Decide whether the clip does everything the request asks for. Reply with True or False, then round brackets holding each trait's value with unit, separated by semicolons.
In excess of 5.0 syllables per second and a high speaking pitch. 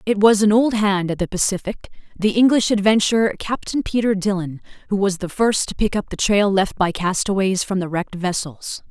True (5.4 syllables/s; 200 Hz)